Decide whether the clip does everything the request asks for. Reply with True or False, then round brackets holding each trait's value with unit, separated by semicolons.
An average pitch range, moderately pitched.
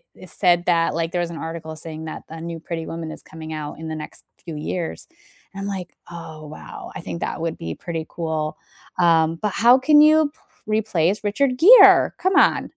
True (3.9 semitones; 165 Hz)